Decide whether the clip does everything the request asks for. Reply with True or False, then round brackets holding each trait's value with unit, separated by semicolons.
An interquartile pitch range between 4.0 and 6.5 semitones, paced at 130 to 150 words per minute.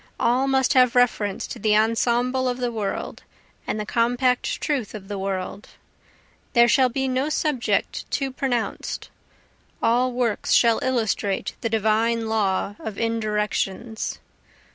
False (2.9 semitones; 135 wpm)